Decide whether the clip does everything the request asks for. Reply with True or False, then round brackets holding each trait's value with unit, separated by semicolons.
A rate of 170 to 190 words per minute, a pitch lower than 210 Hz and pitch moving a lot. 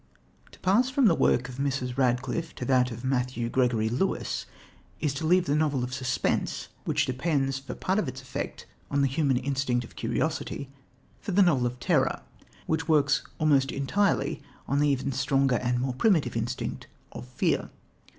False (175 wpm; 135 Hz; 3.5 semitones)